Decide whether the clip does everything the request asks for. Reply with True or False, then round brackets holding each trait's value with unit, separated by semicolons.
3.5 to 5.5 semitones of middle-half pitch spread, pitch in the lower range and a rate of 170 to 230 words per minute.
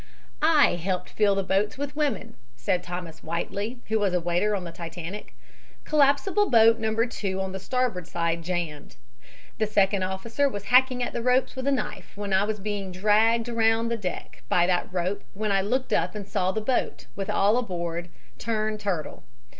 False (4.0 semitones; 205 Hz; 185 wpm)